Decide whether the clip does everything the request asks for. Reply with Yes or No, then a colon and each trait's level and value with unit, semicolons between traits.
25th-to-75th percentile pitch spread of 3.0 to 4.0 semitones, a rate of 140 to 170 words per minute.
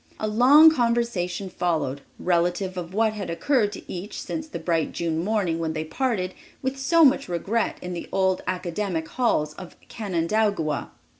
No: average, 5.3 semitones; average, 160 wpm